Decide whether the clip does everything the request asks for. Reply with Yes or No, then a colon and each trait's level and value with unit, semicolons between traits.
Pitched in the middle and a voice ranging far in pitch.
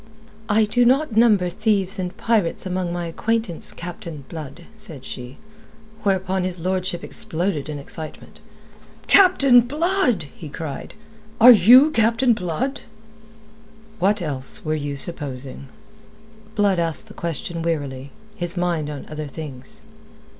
Yes: medium, 180 Hz; wide, 5.9 semitones